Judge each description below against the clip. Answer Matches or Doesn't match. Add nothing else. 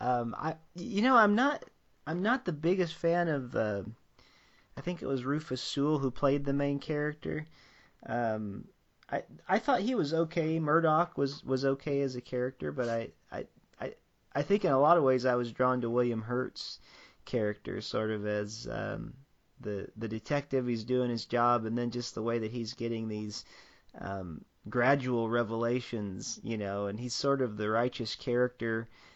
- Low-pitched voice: Matches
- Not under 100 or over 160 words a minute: Doesn't match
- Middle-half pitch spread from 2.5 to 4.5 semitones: Matches